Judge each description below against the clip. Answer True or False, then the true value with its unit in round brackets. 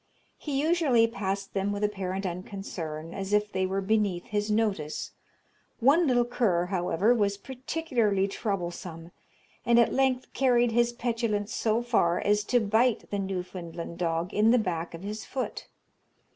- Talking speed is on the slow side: False (150 wpm)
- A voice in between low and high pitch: False (205 Hz)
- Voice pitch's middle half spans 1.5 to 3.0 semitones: False (4.3 semitones)